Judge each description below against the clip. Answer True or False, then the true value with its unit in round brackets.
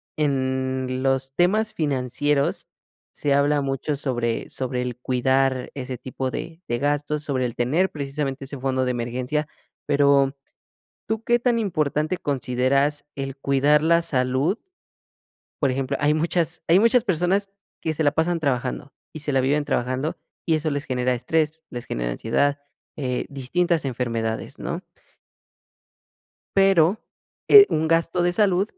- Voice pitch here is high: False (140 Hz)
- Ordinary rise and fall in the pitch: True (3.7 semitones)